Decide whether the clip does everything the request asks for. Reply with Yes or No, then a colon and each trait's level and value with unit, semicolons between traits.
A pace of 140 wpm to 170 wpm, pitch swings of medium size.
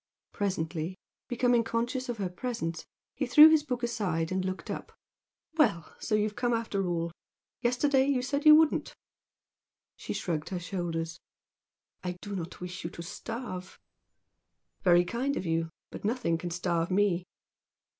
No: average, 150 wpm; wide, 6.0 semitones